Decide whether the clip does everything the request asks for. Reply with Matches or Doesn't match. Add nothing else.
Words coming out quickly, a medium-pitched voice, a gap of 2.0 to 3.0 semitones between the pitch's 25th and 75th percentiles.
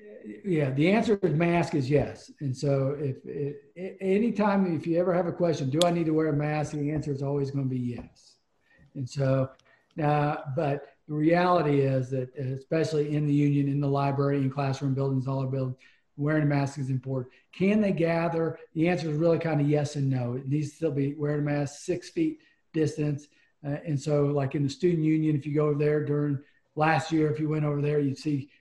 Matches